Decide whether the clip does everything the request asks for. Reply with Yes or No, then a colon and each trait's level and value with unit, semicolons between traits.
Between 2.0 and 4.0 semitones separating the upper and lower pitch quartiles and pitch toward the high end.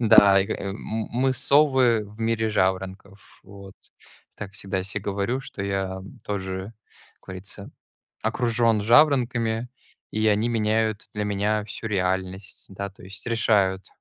No: average, 2.9 semitones; low, 105 Hz